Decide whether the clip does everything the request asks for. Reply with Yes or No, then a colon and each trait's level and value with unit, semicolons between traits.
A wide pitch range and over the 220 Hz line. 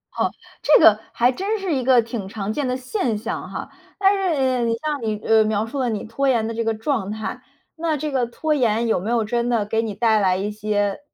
No: average, 3.7 semitones; high, 230 Hz